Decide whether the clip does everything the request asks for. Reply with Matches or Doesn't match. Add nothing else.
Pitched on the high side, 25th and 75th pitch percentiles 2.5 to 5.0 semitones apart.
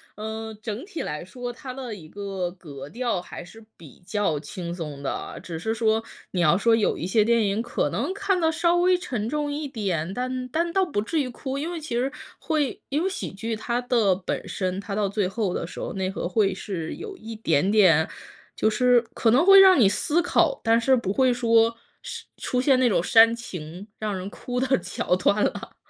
Doesn't match